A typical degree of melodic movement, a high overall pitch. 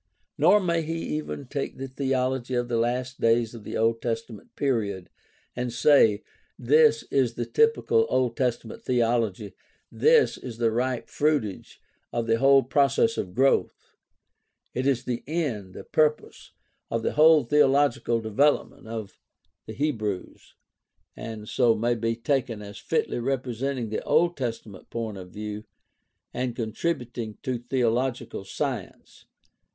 No: average, 3.5 semitones; low, 120 Hz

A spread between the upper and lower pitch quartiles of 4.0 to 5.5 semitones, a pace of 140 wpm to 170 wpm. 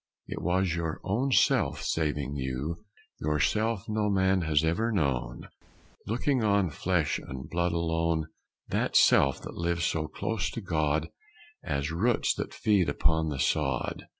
Yes: average, 4.6 semitones; average, 150 wpm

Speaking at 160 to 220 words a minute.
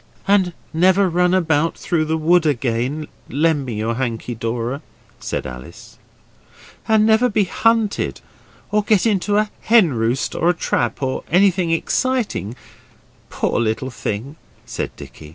No: average, 140 wpm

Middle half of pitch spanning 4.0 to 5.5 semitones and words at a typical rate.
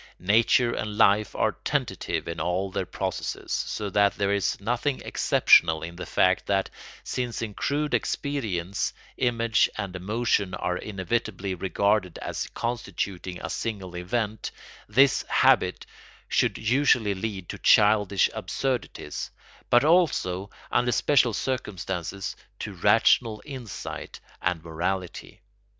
No: average, 4.3 semitones; slow, 120 wpm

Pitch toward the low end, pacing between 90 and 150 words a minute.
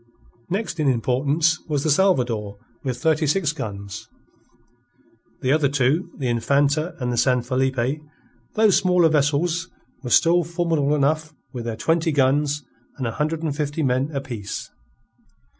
No: medium, 145 Hz; average, 140 wpm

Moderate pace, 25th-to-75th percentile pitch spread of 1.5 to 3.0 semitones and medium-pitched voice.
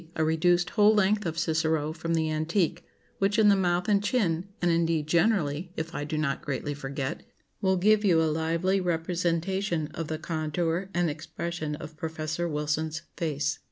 Yes: average, 170 wpm; narrow, 2.5 semitones; medium, 165 Hz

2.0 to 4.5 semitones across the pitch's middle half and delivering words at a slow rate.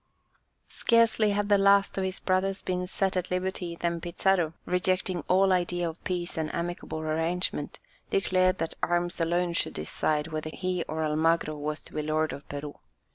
No: average, 2.7 semitones; average, 170 wpm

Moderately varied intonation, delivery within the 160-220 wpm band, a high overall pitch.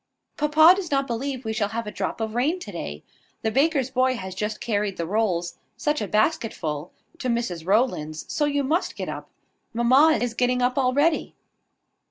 Yes: average, 4.9 semitones; average, 190 wpm; high, 240 Hz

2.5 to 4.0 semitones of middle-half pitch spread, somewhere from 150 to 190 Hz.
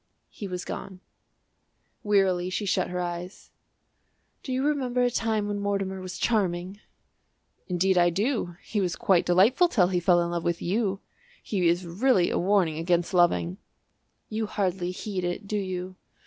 Yes: average, 2.8 semitones; medium, 185 Hz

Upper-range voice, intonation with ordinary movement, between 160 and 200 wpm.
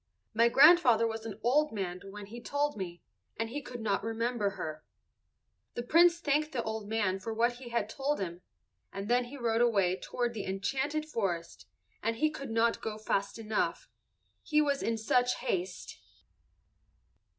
Yes: high, 230 Hz; average, 4.3 semitones; average, 170 wpm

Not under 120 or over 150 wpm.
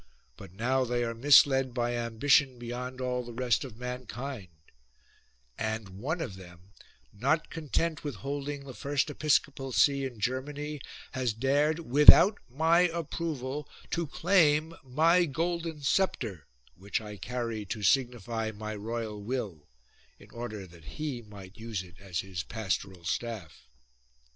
Yes: average, 140 wpm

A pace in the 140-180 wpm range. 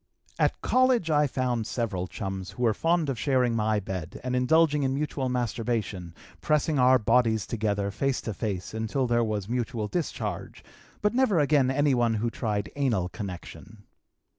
Yes: average, 160 wpm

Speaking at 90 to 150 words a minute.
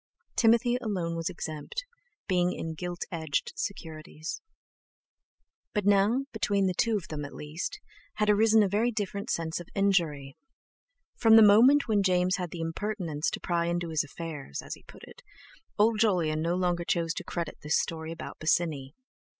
No: average, 160 wpm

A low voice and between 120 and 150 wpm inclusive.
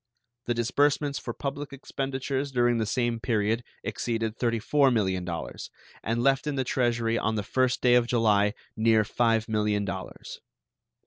Yes: low, 120 Hz; average, 140 wpm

